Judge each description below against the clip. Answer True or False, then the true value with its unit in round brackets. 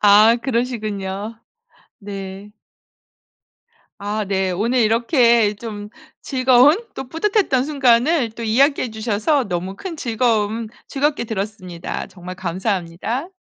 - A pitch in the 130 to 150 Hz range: False (220 Hz)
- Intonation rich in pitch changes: False (4.0 semitones)